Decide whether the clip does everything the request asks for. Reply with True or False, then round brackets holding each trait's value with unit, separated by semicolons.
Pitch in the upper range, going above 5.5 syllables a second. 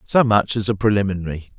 False (105 Hz; 6.2 syllables/s)